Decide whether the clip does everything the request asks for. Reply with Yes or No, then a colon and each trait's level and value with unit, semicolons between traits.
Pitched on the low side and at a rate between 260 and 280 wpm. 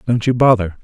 No: low, 115 Hz; fast, 215 wpm